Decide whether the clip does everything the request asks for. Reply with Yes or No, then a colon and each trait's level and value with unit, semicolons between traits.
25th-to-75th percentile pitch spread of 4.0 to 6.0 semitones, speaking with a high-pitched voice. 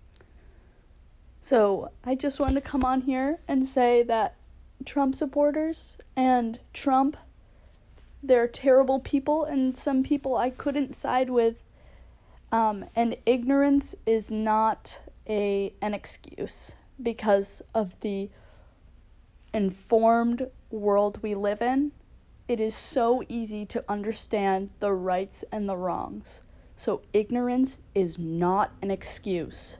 Yes: average, 4.6 semitones; high, 230 Hz